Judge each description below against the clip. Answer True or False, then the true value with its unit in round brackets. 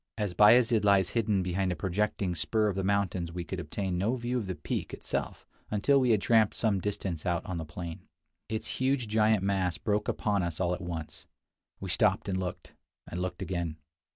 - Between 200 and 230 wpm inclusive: True (205 wpm)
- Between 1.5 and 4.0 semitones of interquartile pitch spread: True (3.2 semitones)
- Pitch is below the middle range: True (95 Hz)